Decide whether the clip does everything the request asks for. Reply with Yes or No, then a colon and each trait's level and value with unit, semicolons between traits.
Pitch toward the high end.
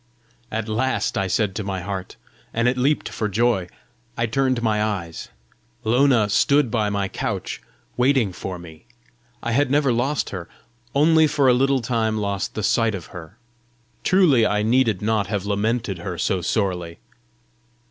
No: low, 110 Hz